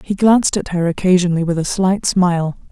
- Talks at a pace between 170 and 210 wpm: Yes, average, 200 wpm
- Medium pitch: Yes, medium, 180 Hz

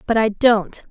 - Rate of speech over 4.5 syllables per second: No, 4.3 syllables/s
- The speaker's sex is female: Yes, female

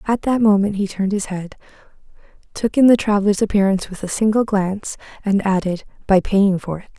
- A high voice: Yes, high, 200 Hz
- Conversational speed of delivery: Yes, average, 190 wpm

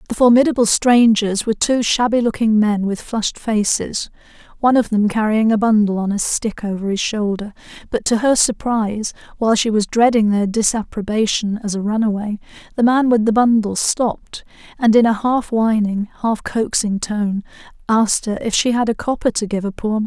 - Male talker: No, female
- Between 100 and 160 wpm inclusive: No, average, 185 wpm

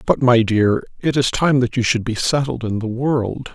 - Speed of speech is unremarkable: No, fast, 235 wpm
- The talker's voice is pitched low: Yes, low, 125 Hz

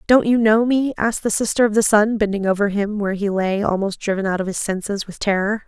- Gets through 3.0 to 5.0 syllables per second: No, 6.0 syllables/s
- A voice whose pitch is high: Yes, high, 210 Hz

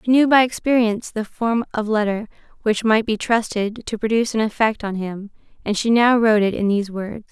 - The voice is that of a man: No, female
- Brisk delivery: Yes, fast, 215 wpm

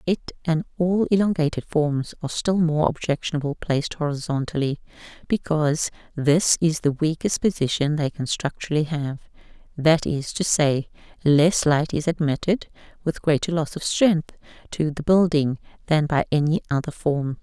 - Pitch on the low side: No, medium, 155 Hz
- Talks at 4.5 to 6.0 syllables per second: Yes, 4.8 syllables/s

